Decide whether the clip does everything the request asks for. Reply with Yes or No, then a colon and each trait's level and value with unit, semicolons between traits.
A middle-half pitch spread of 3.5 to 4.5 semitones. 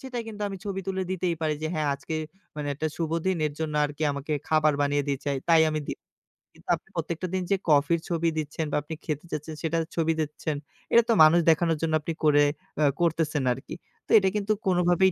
No: average, 2.8 semitones